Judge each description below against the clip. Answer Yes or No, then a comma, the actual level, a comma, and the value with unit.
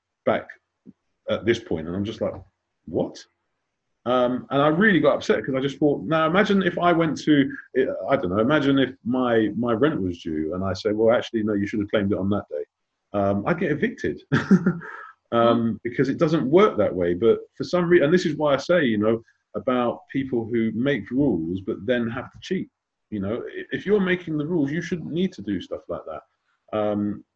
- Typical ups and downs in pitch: No, wide, 7.9 semitones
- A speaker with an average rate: No, fast, 215 wpm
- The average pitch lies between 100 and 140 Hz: Yes, low, 135 Hz